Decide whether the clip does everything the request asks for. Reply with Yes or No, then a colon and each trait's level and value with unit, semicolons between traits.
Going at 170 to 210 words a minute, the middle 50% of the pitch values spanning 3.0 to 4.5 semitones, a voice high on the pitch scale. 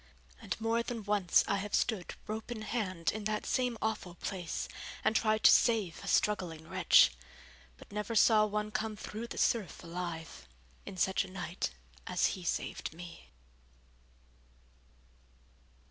No: average, 145 wpm; average, 3.6 semitones; high, 210 Hz